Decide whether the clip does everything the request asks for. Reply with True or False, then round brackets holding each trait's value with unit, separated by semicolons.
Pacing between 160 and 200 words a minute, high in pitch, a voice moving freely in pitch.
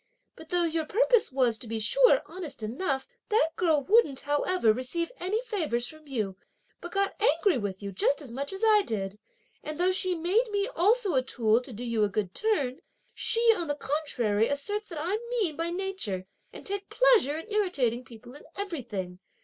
True (190 wpm; 310 Hz; 8.3 semitones)